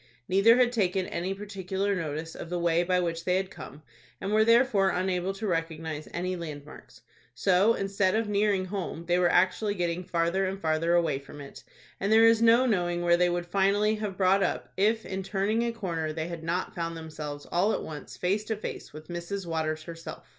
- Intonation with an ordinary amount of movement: Yes, average, 3.2 semitones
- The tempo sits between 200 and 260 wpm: Yes, fast, 205 wpm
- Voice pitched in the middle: Yes, medium, 180 Hz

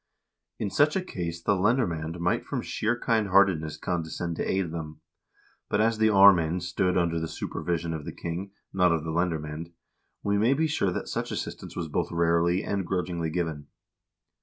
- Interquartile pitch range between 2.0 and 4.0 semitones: Yes, average, 3.2 semitones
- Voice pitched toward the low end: Yes, very low, 90 Hz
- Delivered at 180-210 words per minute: Yes, average, 185 wpm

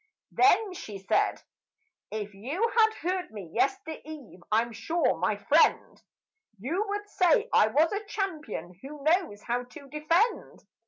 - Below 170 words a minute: Yes, average, 140 wpm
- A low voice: No, very high, 300 Hz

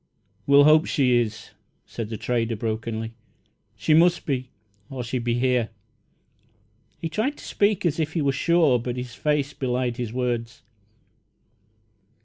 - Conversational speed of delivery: Yes, average, 145 wpm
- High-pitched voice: No, low, 125 Hz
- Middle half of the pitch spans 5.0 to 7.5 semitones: No, average, 4.5 semitones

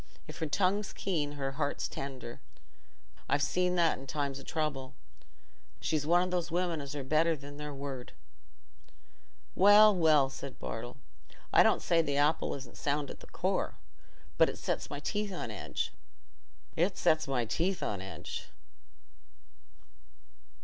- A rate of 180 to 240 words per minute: No, average, 150 wpm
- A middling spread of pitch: Yes, average, 4.0 semitones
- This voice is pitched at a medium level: Yes, medium, 145 Hz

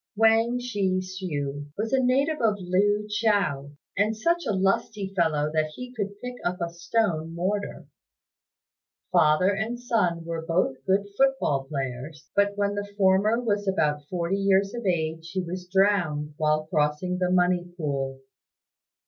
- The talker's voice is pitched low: No, medium, 185 Hz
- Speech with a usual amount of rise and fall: Yes, average, 4.6 semitones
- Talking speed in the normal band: Yes, average, 155 wpm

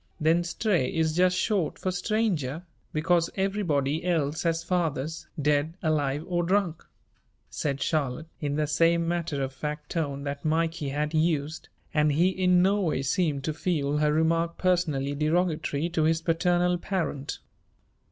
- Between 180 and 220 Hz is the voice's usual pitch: No, medium, 160 Hz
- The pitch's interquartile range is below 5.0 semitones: Yes, average, 2.9 semitones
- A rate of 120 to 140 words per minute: No, average, 150 wpm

